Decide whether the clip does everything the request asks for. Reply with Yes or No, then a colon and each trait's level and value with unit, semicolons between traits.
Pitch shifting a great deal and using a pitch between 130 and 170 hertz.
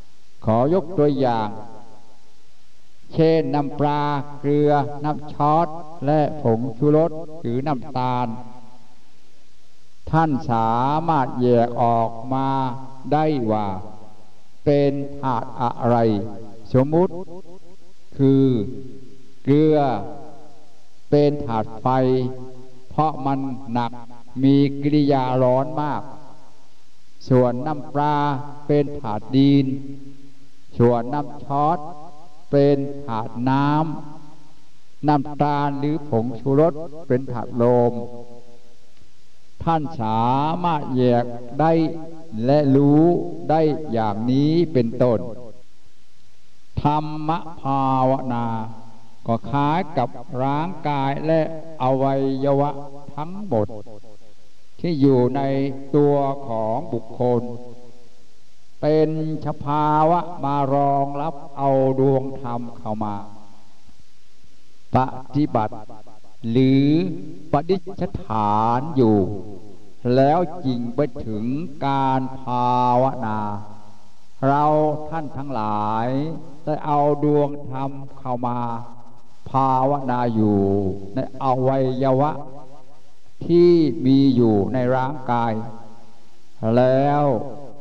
No: average, 3.6 semitones; low, 135 Hz